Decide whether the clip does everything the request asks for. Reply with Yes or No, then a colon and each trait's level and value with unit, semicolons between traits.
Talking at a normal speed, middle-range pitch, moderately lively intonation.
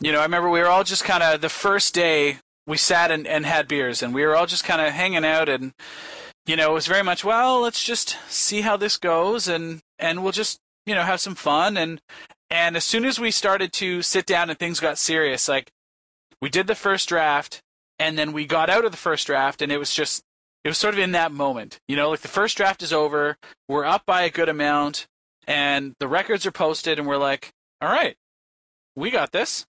No: fast, 240 wpm; medium, 165 Hz; average, 4.1 semitones